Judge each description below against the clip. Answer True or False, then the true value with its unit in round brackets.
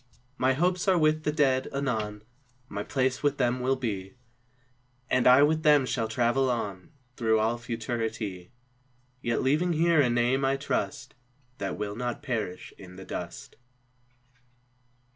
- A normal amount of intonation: True (4.1 semitones)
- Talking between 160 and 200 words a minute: False (145 wpm)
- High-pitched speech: False (125 Hz)